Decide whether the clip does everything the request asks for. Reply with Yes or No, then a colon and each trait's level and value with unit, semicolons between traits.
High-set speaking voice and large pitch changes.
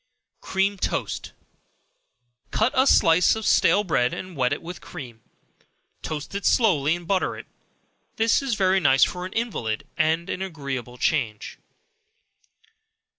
No: medium, 175 Hz; wide, 6.2 semitones